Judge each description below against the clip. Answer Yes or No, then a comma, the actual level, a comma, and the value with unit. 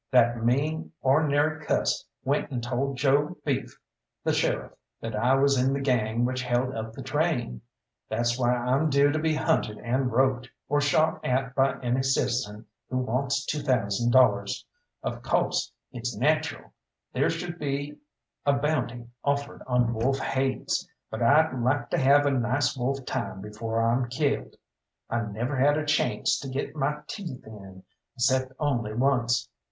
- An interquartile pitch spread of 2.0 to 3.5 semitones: Yes, average, 3.1 semitones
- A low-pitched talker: Yes, low, 130 Hz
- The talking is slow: No, average, 160 wpm